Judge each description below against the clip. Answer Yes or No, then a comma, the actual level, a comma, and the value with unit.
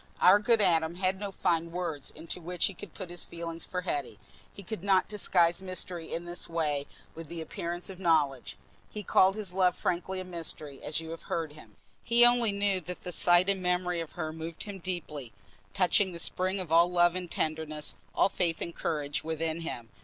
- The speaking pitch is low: No, medium, 175 Hz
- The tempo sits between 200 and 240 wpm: Yes, fast, 205 wpm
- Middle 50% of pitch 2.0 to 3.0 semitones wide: Yes, narrow, 2.4 semitones